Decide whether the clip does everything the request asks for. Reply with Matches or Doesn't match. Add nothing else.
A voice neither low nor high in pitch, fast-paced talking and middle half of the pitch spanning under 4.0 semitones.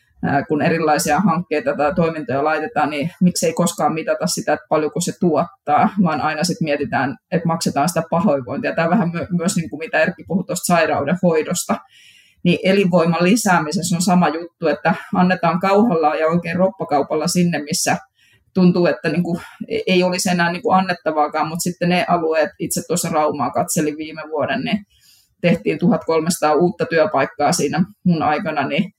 Matches